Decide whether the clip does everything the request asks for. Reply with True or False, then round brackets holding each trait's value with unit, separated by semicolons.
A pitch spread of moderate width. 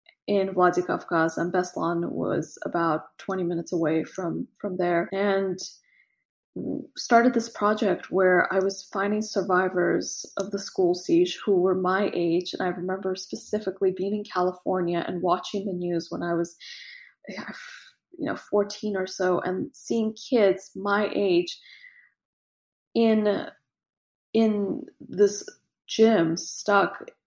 True (3.4 semitones)